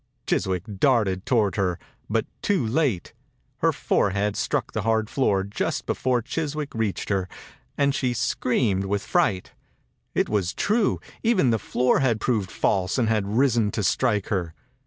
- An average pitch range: Yes, average, 4.7 semitones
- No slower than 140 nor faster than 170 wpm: Yes, average, 155 wpm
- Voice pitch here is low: Yes, low, 110 Hz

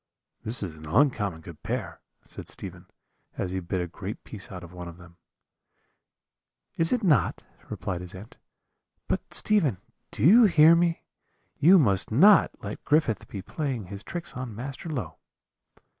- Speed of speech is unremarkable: Yes, average, 160 wpm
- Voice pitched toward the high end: No, low, 110 Hz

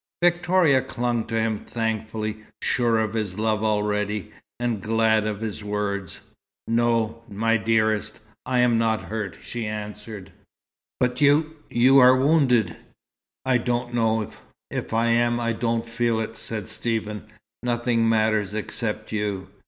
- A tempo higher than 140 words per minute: No, slow, 135 wpm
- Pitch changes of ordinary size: No, narrow, 1.9 semitones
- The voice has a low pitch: Yes, low, 115 Hz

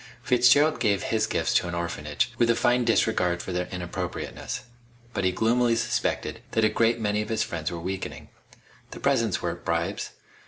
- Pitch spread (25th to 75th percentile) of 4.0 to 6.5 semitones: Yes, average, 4.7 semitones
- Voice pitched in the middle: No, low, 110 Hz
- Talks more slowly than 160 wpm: No, average, 180 wpm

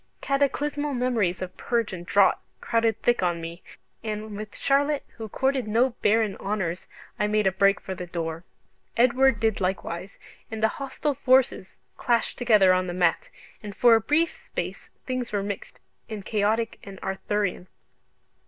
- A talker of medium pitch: No, high, 215 Hz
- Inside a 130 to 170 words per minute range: Yes, average, 160 wpm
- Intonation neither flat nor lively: Yes, average, 4.3 semitones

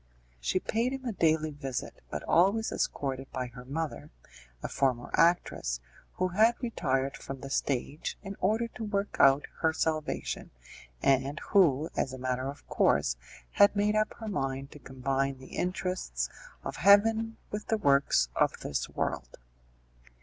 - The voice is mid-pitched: Yes, medium, 150 Hz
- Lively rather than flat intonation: Yes, wide, 7.1 semitones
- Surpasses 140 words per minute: Yes, average, 155 wpm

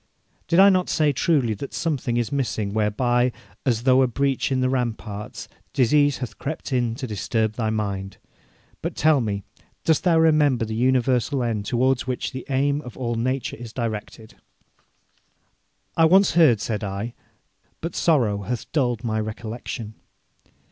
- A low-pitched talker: Yes, low, 125 Hz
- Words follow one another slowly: No, average, 155 wpm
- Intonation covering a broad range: No, average, 4.1 semitones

